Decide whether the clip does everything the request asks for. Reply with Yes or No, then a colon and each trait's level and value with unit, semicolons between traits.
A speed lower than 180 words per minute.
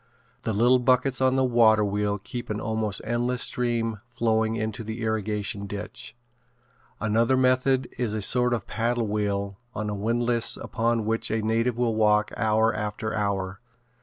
Yes: average, 160 wpm